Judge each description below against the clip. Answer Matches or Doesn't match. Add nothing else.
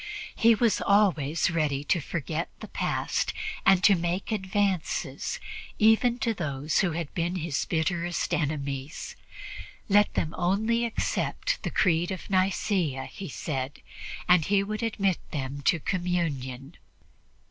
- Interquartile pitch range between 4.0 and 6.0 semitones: Matches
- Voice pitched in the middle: Matches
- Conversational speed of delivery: Doesn't match